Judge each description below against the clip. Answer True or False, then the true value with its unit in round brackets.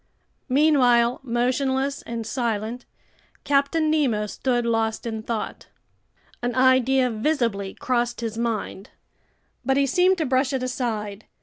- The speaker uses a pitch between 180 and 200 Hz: False (245 Hz)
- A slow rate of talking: True (120 wpm)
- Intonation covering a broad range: False (2.9 semitones)